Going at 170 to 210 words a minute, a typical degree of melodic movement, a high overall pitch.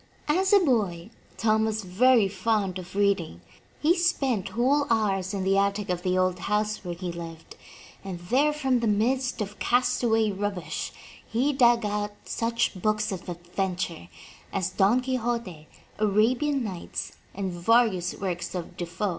No: average, 155 wpm; average, 4.5 semitones; high, 210 Hz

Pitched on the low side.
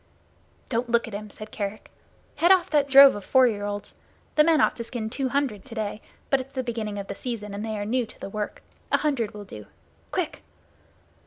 No: high, 230 Hz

